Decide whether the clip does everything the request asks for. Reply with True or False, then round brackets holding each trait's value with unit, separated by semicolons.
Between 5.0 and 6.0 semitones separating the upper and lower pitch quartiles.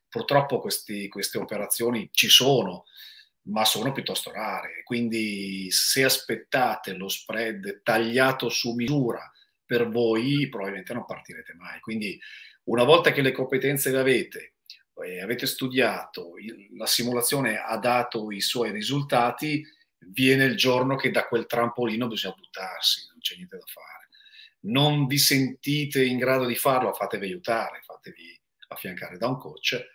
False (3.1 semitones)